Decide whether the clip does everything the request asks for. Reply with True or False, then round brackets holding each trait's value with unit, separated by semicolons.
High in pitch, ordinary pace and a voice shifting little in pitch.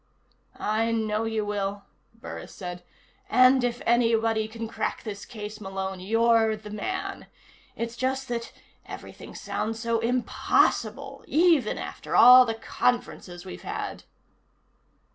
False (225 Hz; 125 wpm; 2.1 semitones)